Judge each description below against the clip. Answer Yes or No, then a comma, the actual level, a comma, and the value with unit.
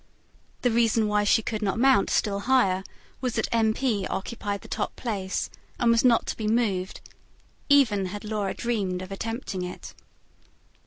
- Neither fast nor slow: Yes, average, 165 wpm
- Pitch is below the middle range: No, high, 215 Hz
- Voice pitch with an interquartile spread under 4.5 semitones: Yes, average, 3.0 semitones